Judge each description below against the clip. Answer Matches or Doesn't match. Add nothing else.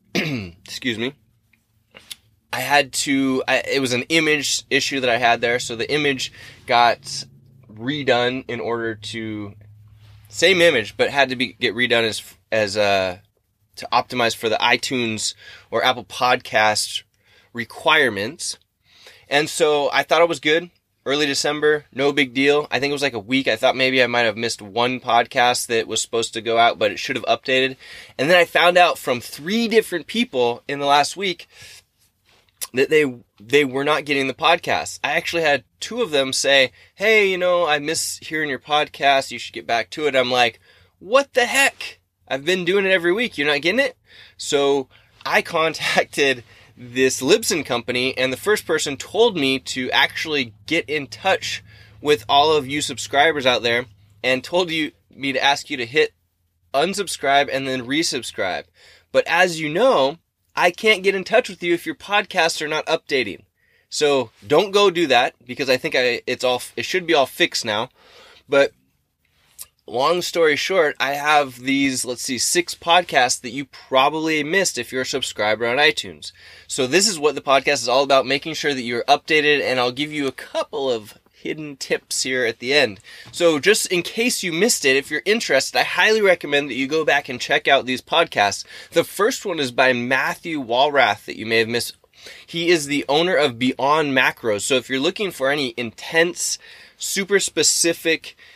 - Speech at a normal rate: Matches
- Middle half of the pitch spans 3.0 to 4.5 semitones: Doesn't match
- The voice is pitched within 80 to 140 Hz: Matches